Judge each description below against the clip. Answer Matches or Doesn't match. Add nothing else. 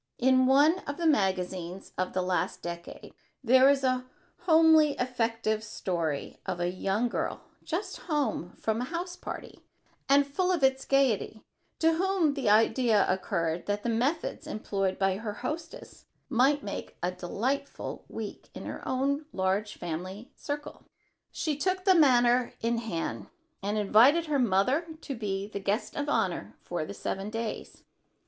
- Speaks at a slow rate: Doesn't match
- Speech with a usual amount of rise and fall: Doesn't match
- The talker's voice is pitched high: Matches